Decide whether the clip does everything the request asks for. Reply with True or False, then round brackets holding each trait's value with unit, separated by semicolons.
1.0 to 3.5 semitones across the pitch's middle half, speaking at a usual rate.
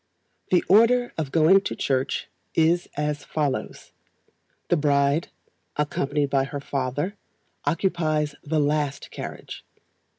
False (2.9 semitones; 110 wpm)